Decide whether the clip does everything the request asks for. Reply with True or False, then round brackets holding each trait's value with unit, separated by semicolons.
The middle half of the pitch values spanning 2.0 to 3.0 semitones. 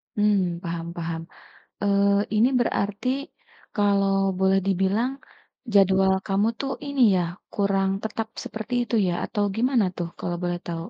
True (2.5 semitones)